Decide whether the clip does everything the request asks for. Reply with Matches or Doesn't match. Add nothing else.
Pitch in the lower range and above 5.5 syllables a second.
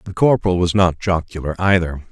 Matches